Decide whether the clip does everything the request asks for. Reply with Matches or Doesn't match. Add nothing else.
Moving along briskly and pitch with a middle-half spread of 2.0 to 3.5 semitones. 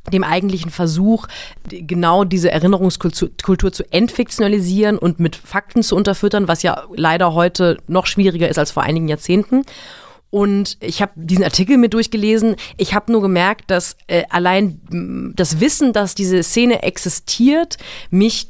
Doesn't match